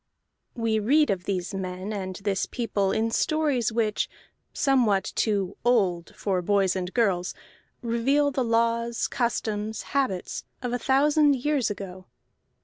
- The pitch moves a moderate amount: Yes, average, 4.3 semitones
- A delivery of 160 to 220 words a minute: No, slow, 135 wpm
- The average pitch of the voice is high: Yes, high, 220 Hz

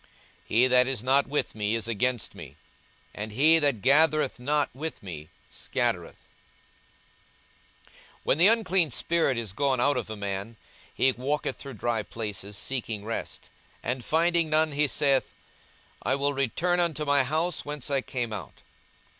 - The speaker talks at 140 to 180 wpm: Yes, average, 160 wpm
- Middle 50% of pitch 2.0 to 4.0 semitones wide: No, average, 4.7 semitones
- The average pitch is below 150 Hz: Yes, low, 135 Hz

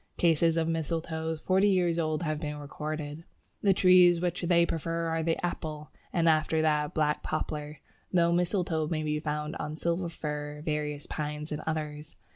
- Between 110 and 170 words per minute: Yes, average, 165 wpm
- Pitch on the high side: No, medium, 160 Hz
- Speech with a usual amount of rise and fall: No, narrow, 2.0 semitones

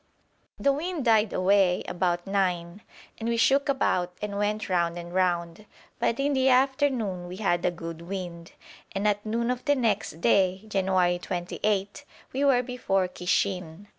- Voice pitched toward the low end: No, high, 195 Hz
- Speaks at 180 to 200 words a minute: No, average, 160 wpm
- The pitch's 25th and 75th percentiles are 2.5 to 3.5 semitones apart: No, average, 4.8 semitones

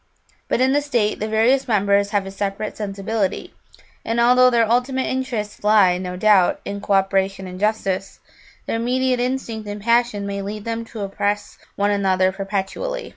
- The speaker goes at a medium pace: Yes, average, 170 wpm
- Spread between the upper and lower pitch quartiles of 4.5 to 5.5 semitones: No, average, 3.3 semitones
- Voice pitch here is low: No, high, 210 Hz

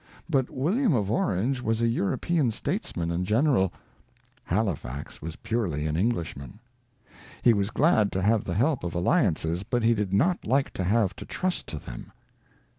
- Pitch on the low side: Yes, low, 105 Hz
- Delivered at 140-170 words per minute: Yes, average, 165 wpm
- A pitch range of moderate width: No, wide, 6.5 semitones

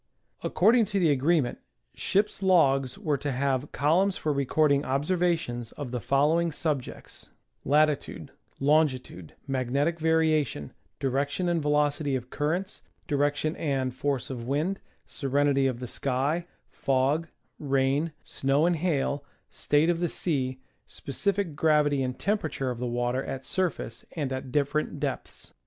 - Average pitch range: Yes, average, 3.4 semitones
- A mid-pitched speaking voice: Yes, medium, 145 Hz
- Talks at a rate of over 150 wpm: No, average, 140 wpm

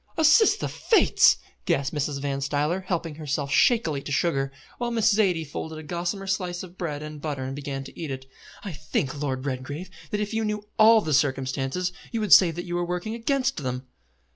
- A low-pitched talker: No, medium, 160 Hz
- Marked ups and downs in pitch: Yes, wide, 5.7 semitones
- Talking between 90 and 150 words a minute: No, average, 200 wpm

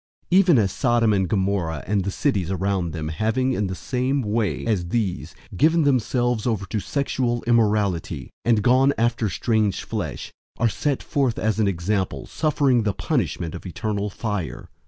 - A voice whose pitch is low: Yes, low, 110 Hz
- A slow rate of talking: No, average, 165 wpm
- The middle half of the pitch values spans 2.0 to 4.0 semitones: No, average, 4.4 semitones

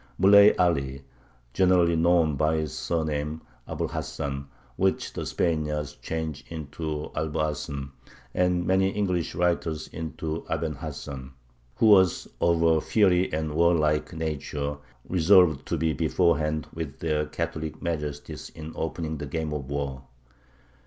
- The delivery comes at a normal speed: No, slow, 130 wpm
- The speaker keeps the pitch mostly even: Yes, narrow, 2.3 semitones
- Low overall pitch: Yes, very low, 80 Hz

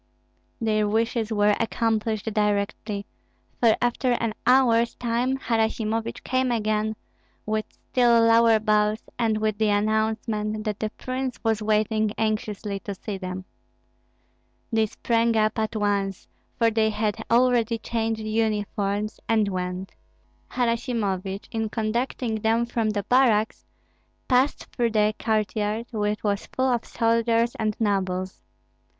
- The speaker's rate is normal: No, slow, 125 wpm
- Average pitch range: No, narrow, 1.6 semitones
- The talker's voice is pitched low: No, high, 220 Hz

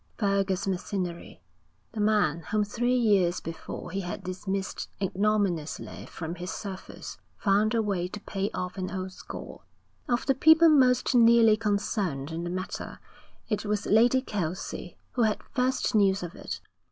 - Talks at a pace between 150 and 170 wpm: Yes, average, 155 wpm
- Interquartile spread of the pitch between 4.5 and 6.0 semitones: No, average, 3.3 semitones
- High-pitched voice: Yes, high, 200 Hz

